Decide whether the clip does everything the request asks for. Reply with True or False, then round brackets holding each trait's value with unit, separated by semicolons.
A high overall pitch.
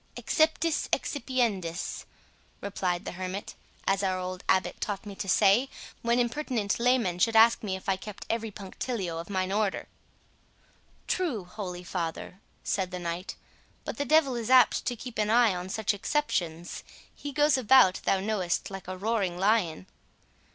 True (200 Hz)